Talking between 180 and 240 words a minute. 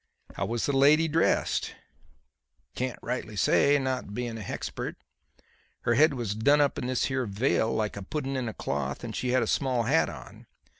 Yes: average, 190 wpm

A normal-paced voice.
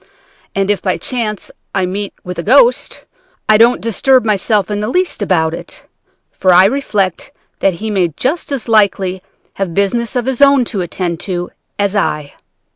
Yes: average, 175 wpm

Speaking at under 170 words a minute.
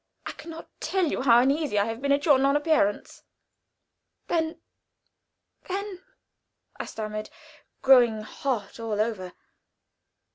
Yes: slow, 135 wpm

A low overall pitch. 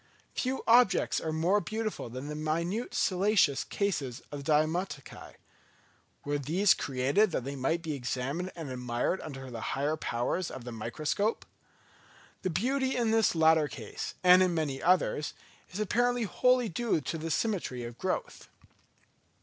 No: medium, 160 Hz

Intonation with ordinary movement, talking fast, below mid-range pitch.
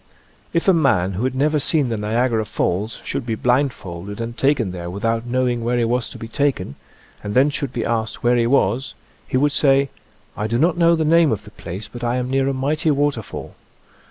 Yes: average, 4.2 semitones; fast, 225 wpm; low, 120 Hz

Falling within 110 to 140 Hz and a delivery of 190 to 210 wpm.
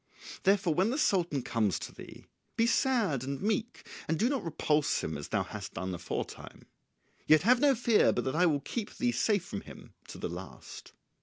No: medium, 180 Hz; average, 200 wpm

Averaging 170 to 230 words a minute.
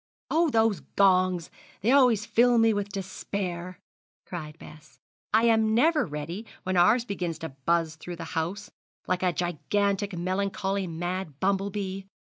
No: average, 145 wpm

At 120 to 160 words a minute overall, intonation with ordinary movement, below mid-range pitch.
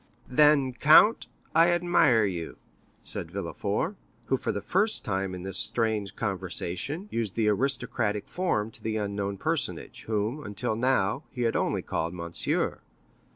No: average, 145 wpm; wide, 5.7 semitones; low, 110 Hz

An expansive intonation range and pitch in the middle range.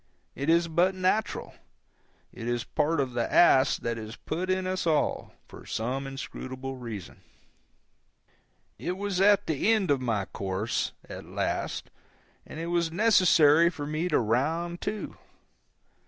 Yes: wide, 6.0 semitones; medium, 155 Hz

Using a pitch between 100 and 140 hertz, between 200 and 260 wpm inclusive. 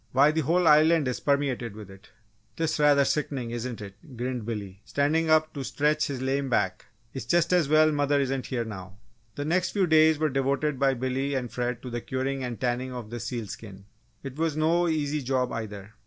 Yes: low, 135 Hz; fast, 205 wpm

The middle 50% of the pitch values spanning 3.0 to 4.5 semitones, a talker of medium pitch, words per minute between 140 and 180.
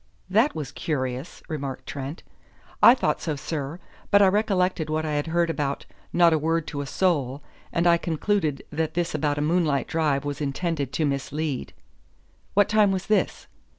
Yes: average, 3.5 semitones; medium, 155 Hz; average, 175 wpm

